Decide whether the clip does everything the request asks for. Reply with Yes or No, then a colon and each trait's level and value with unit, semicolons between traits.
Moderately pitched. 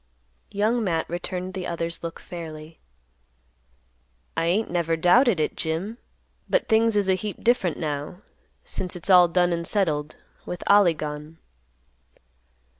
Yes: medium, 175 Hz